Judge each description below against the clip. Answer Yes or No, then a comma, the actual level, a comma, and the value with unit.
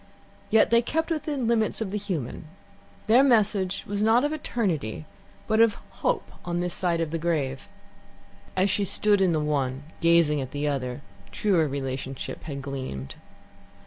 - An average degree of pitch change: No, wide, 7.4 semitones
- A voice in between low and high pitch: Yes, medium, 175 Hz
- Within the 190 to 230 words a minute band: No, average, 160 wpm